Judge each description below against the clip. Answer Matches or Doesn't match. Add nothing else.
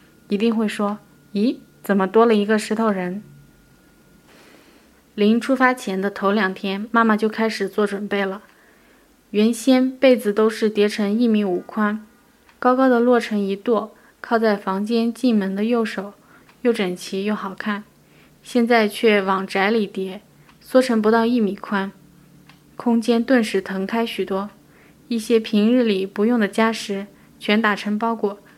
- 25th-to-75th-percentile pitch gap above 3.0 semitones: Doesn't match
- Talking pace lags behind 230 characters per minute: Matches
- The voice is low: Doesn't match